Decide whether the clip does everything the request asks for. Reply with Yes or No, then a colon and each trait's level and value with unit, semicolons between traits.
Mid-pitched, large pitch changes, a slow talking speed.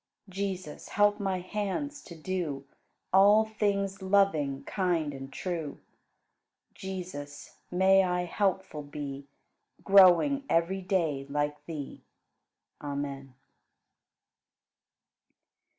No: medium, 180 Hz; average, 4.9 semitones; slow, 85 wpm